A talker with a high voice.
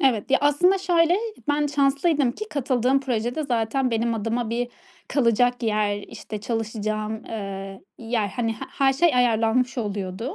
Yes: high, 240 Hz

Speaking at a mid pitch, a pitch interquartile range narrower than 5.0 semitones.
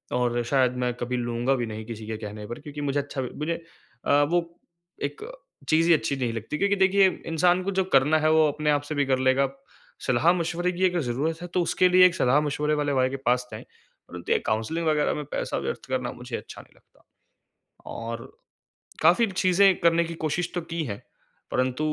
No: medium, 150 Hz; average, 5.3 semitones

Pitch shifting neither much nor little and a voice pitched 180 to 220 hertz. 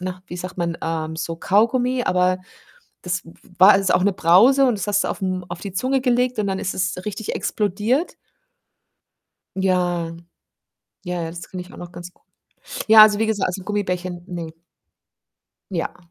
Yes: average, 3.0 semitones; medium, 185 Hz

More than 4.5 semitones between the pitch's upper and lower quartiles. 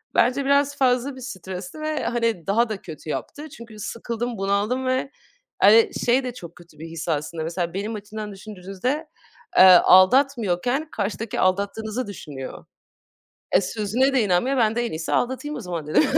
Yes: wide, 5.4 semitones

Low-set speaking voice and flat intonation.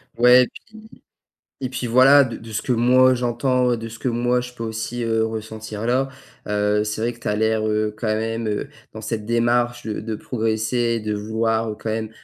Yes: low, 115 Hz; narrow, 1.9 semitones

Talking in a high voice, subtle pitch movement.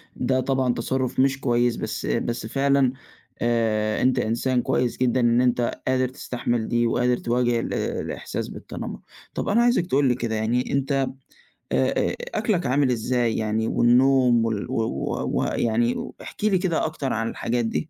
No: low, 125 Hz; narrow, 2.2 semitones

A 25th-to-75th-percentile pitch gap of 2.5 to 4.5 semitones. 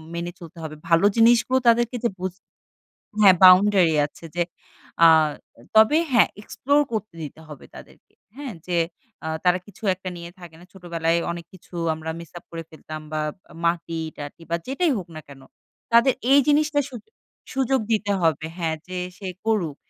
No: wide, 5.6 semitones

